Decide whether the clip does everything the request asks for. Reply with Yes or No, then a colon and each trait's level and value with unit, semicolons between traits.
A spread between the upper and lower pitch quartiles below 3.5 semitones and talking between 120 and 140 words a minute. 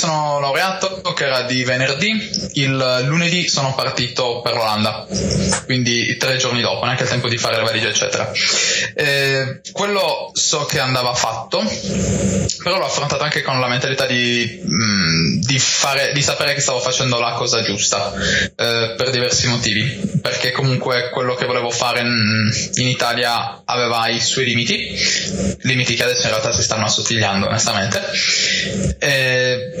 No: narrow, 2.5 semitones; average, 150 wpm